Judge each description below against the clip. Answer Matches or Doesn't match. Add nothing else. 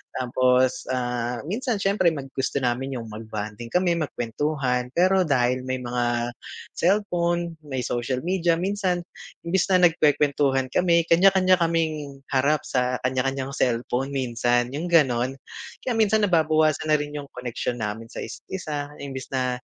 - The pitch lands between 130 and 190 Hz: Matches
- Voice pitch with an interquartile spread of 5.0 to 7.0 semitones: Matches